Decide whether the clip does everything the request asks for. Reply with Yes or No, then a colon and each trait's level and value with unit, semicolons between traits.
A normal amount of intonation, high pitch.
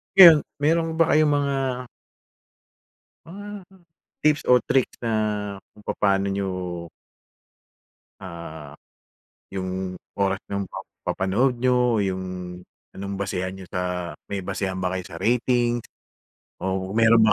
No: average, 4.9 semitones; low, 100 Hz